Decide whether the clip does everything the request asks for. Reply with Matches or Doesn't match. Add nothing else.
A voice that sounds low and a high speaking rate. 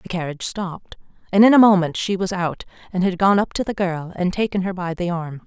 Doesn't match